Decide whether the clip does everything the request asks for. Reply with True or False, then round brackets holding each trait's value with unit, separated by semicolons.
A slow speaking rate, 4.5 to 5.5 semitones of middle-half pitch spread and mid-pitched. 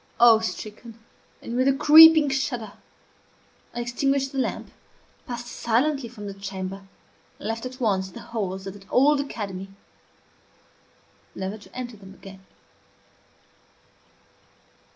False (125 wpm; 4.8 semitones; 230 Hz)